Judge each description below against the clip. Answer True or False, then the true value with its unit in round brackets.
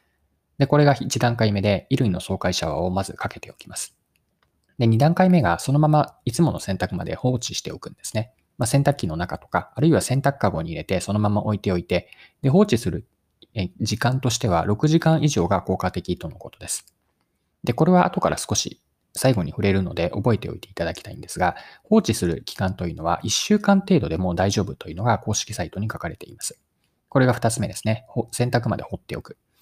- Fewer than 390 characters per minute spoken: False (395 characters per minute)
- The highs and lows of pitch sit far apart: True (5.8 semitones)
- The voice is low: True (105 Hz)